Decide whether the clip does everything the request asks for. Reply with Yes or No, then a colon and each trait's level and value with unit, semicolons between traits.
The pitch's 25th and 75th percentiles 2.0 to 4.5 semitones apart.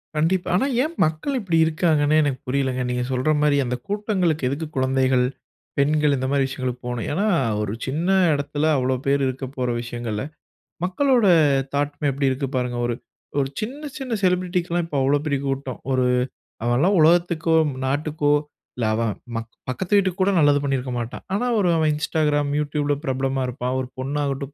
Yes: average, 4.1 semitones